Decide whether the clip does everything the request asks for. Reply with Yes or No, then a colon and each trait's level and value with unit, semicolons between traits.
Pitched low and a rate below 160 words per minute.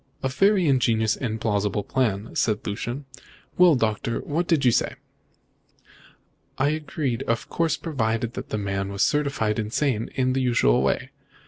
Yes: low, 120 Hz; average, 150 wpm